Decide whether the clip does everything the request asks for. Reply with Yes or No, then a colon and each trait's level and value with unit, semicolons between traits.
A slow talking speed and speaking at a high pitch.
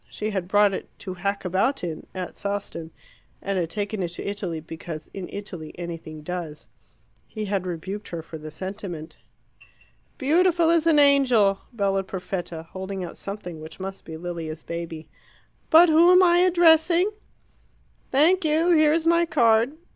No: average, 160 wpm; high, 195 Hz